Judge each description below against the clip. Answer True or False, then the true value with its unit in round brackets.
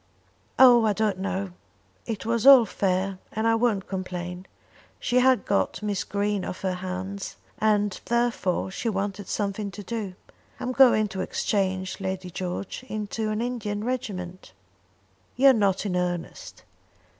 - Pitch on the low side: False (200 Hz)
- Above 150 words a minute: False (145 wpm)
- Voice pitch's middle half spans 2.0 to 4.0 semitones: True (3.1 semitones)